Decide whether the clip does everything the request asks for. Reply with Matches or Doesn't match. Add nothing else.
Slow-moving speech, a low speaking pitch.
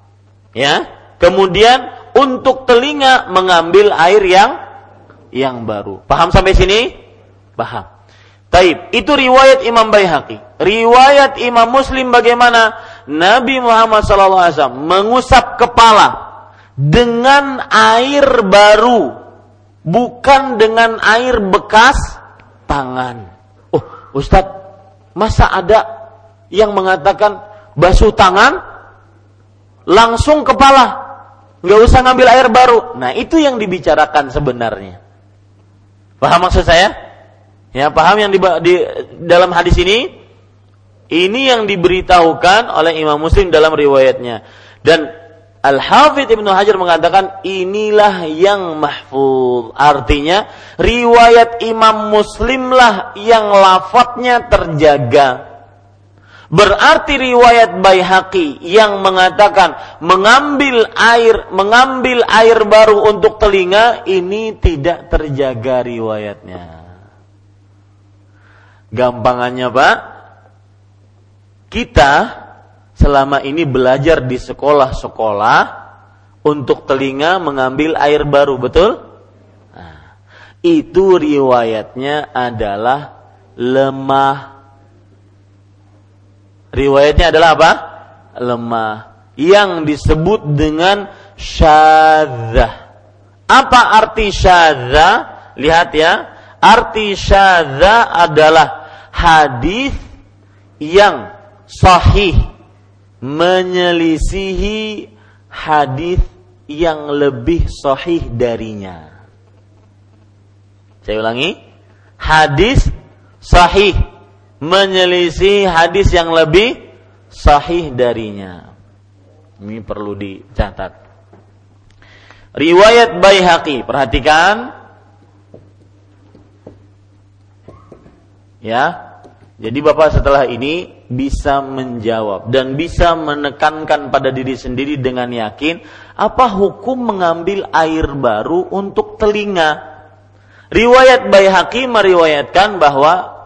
Doesn't match